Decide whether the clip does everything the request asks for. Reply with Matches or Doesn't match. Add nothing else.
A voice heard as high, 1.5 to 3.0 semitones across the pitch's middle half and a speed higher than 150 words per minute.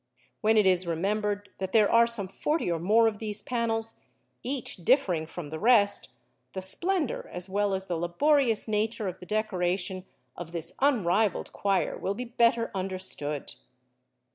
Doesn't match